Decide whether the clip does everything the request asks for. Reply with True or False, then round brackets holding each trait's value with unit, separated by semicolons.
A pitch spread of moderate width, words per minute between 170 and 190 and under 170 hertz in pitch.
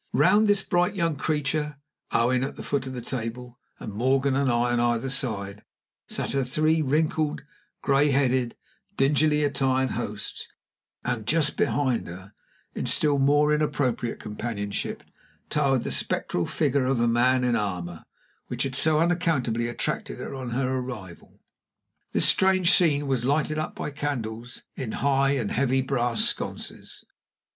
False (3.7 semitones; 150 wpm; 135 Hz)